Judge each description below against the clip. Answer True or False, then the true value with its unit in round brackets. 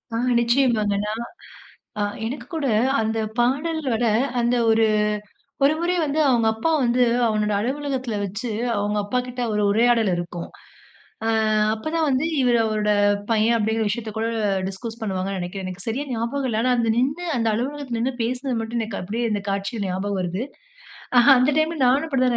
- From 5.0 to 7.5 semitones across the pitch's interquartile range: False (3.5 semitones)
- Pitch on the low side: False (235 Hz)